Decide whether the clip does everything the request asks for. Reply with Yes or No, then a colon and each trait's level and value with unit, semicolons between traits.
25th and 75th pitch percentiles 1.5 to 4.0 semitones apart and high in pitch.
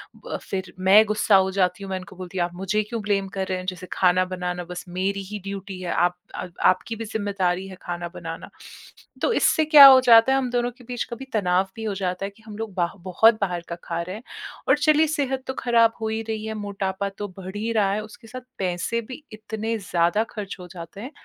Yes: average, 3.6 semitones; high, 200 Hz